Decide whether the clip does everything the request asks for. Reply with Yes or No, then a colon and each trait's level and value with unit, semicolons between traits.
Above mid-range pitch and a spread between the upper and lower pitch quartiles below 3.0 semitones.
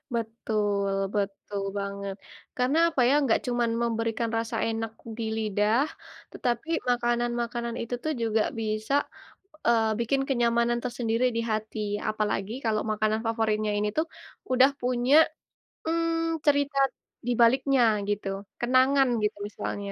Yes: high, 235 Hz; narrow, 2.6 semitones